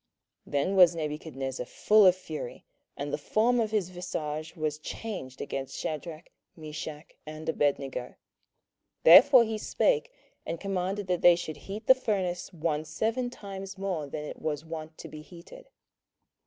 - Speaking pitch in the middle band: Yes, medium, 170 Hz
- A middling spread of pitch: Yes, average, 4.5 semitones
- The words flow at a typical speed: Yes, average, 155 wpm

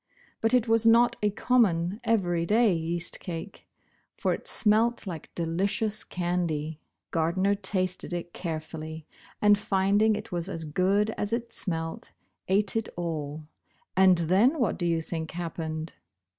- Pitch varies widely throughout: No, average, 4.2 semitones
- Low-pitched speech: No, medium, 185 Hz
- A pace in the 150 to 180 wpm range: No, average, 140 wpm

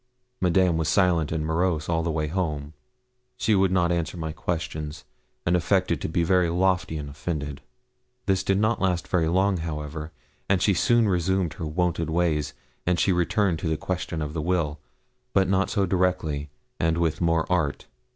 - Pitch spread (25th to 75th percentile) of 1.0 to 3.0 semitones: Yes, average, 2.7 semitones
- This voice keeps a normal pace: Yes, average, 180 wpm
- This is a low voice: Yes, very low, 85 Hz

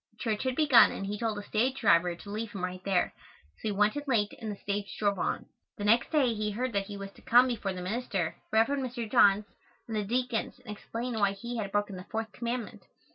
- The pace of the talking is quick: Yes, fast, 235 wpm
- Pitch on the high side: Yes, high, 215 Hz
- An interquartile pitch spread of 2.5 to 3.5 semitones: Yes, average, 3.0 semitones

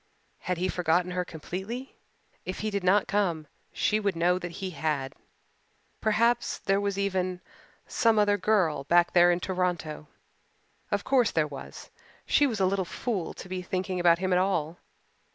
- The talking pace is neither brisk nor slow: Yes, average, 170 wpm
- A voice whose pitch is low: No, medium, 185 Hz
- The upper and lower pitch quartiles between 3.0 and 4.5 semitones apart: No, narrow, 2.6 semitones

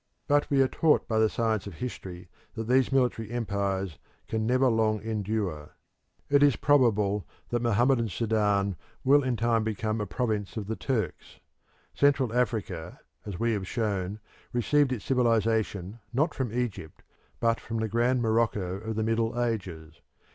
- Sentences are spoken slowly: No, average, 155 wpm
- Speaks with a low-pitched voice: Yes, low, 110 Hz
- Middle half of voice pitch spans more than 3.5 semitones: No, average, 3.1 semitones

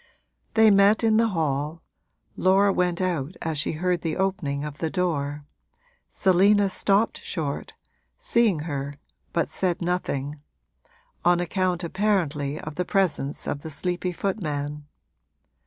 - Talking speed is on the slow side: Yes, slow, 130 wpm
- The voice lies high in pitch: No, medium, 175 Hz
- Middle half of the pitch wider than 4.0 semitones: Yes, average, 4.4 semitones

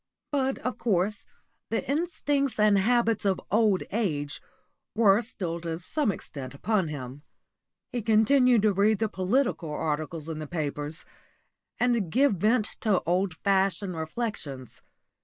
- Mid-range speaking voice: No, high, 200 Hz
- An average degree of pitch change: No, wide, 5.9 semitones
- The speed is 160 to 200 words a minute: No, slow, 135 wpm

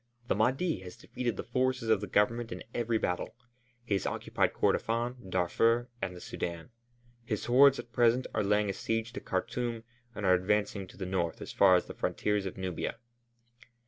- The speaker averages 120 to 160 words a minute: No, average, 185 wpm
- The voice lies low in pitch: Yes, low, 110 Hz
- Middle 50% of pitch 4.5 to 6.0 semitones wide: No, average, 4.0 semitones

